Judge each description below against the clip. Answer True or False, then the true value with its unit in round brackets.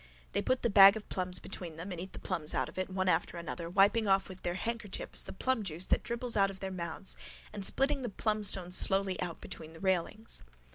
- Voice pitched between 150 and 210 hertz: True (190 Hz)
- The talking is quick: True (225 wpm)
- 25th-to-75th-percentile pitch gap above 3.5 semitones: False (2.8 semitones)